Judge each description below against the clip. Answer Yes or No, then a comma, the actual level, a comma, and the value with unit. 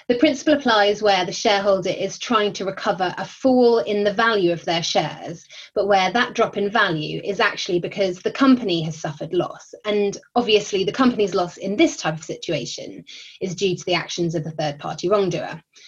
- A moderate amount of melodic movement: Yes, average, 3.6 semitones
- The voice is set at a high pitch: Yes, high, 195 Hz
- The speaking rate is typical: Yes, average, 195 wpm